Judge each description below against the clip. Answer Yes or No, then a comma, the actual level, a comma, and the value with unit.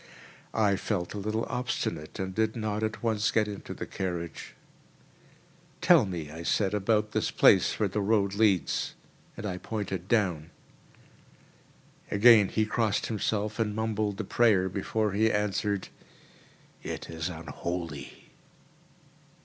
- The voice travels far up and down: No, average, 2.8 semitones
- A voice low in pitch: Yes, low, 105 Hz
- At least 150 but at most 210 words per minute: No, slow, 135 wpm